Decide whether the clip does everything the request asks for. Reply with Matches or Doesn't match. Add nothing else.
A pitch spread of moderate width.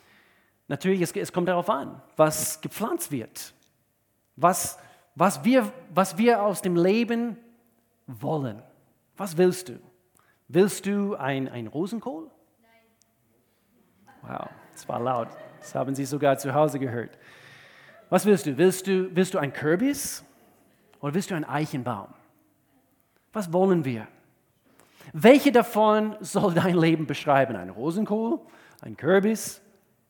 Doesn't match